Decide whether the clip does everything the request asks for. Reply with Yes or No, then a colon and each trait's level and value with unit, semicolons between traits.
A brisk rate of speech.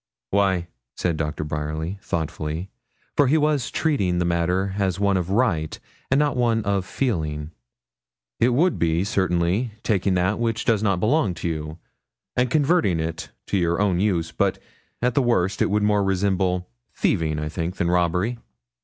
No: average, 160 wpm